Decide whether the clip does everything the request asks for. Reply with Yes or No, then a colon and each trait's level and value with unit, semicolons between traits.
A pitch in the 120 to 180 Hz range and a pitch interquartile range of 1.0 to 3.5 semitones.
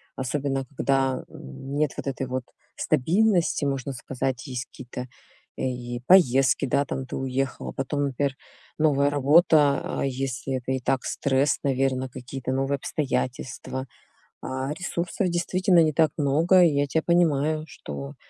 Yes: low, 135 Hz; average, 2.7 semitones